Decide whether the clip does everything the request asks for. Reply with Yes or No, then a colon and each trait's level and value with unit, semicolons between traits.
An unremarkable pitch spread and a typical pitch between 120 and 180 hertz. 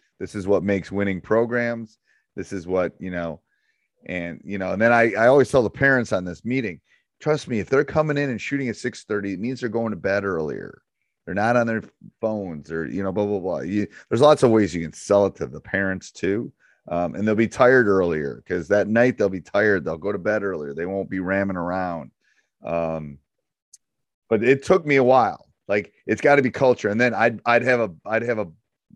No: average, 4.6 semitones; low, 105 Hz